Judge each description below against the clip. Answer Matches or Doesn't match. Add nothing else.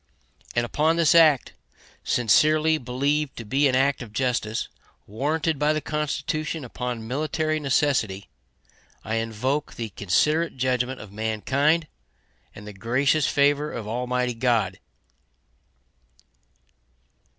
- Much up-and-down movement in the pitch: Doesn't match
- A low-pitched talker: Matches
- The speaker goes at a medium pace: Doesn't match